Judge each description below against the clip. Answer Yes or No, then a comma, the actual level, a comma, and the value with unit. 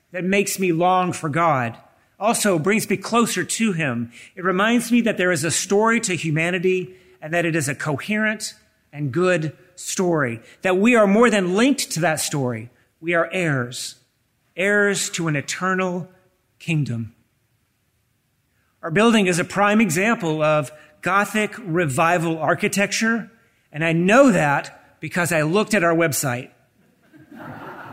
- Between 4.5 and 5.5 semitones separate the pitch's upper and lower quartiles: Yes, average, 5.1 semitones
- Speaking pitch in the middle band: Yes, medium, 175 Hz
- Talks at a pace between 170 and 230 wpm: No, average, 145 wpm